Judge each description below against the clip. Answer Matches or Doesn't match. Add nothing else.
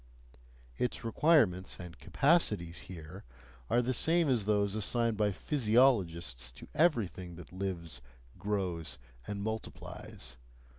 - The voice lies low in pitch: Matches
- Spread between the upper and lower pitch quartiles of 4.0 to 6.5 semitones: Matches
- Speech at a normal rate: Doesn't match